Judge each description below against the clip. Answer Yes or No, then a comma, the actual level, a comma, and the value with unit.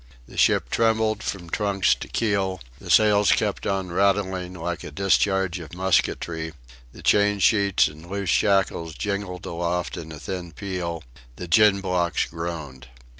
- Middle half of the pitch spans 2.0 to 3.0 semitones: Yes, average, 2.7 semitones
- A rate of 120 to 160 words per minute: Yes, average, 150 wpm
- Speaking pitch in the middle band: No, very low, 95 Hz